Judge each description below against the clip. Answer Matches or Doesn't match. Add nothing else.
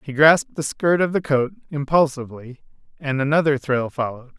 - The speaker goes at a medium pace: Matches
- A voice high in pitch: Doesn't match